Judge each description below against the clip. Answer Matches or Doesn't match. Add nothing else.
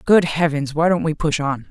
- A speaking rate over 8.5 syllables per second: Doesn't match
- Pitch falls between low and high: Matches